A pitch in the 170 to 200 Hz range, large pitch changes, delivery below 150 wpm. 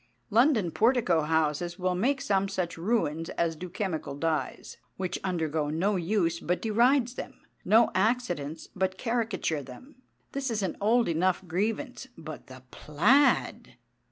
Yes: medium, 185 Hz; wide, 5.7 semitones; average, 140 wpm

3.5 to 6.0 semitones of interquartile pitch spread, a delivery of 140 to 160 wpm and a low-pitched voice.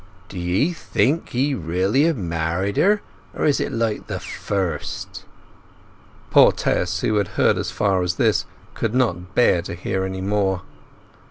Yes: average, 4.8 semitones; average, 145 wpm; very low, 95 Hz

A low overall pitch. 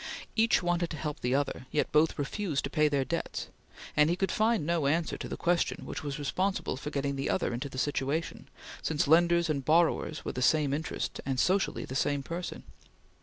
No: medium, 150 Hz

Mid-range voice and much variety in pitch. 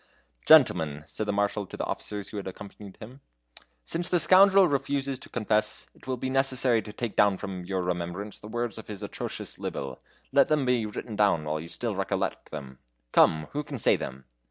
No: low, 105 Hz; wide, 6.1 semitones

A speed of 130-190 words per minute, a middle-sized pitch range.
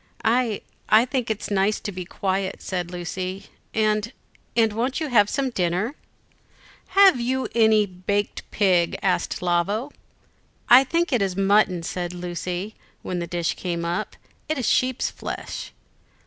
Yes: average, 150 wpm; average, 4.6 semitones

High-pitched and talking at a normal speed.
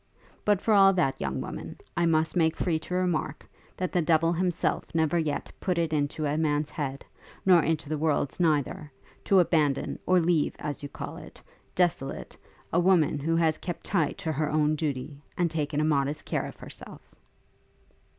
No: medium, 160 Hz; average, 180 wpm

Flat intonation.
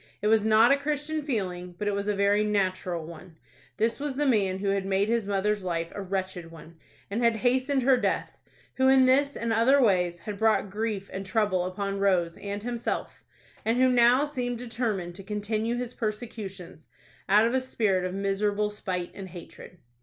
No: average, 4.0 semitones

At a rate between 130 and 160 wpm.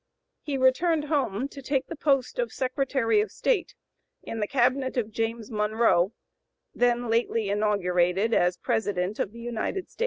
Yes: average, 155 wpm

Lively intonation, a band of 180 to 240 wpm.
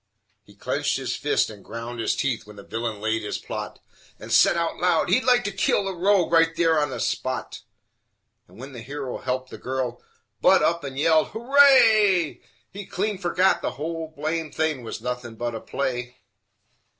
Yes: wide, 6.6 semitones; average, 185 wpm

